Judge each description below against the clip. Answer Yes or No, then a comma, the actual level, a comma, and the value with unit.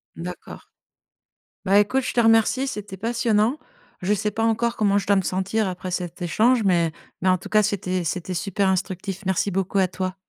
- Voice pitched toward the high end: Yes, high, 195 Hz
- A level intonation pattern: No, average, 3.0 semitones